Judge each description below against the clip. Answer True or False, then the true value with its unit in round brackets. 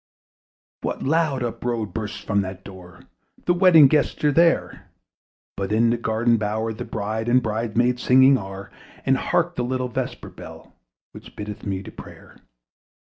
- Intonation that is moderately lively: True (3.8 semitones)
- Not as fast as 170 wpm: True (160 wpm)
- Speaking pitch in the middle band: False (115 Hz)